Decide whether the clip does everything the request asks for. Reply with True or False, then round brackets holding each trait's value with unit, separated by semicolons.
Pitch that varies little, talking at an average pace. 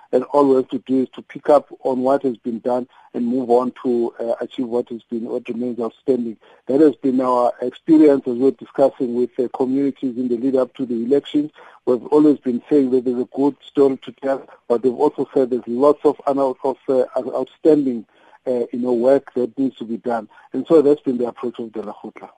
False (2.2 semitones; 225 wpm)